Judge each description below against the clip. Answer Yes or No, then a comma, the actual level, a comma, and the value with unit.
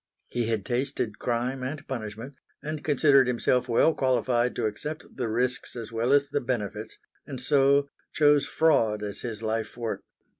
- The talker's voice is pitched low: Yes, low, 125 Hz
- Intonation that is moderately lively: Yes, average, 3.7 semitones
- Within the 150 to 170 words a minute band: Yes, average, 160 wpm